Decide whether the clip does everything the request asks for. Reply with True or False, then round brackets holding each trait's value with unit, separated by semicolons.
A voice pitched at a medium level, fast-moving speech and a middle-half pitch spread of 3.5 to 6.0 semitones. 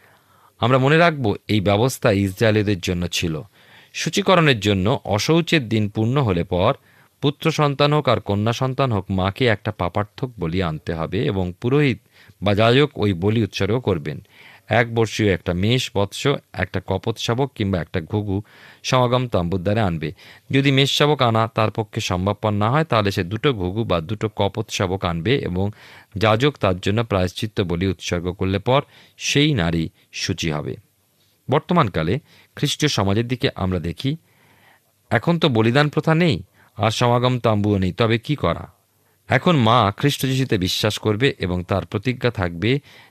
False (110 Hz; 140 wpm; 5.2 semitones)